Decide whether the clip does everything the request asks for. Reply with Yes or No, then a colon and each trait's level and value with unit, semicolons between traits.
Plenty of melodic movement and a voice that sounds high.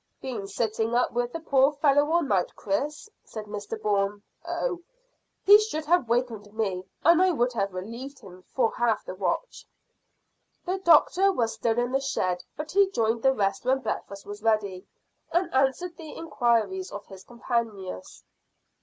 Yes: wide, 6.6 semitones; high, 240 Hz